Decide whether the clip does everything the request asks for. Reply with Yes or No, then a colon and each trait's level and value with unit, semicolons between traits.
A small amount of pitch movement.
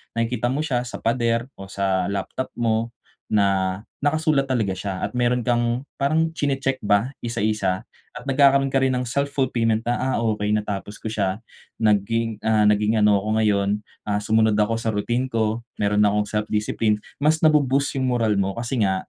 No: average, 3.5 semitones